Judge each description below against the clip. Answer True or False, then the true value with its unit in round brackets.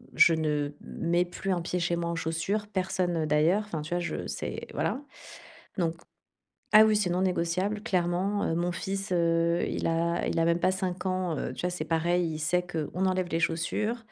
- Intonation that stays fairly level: True (2.0 semitones)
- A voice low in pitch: False (175 Hz)